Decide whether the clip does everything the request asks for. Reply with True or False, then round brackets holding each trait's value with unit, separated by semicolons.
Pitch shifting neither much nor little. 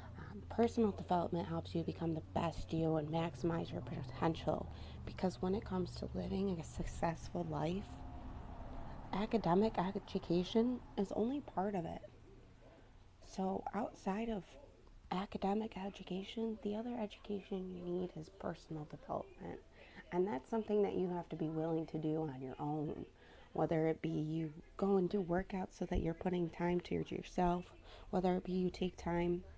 True (3.5 semitones)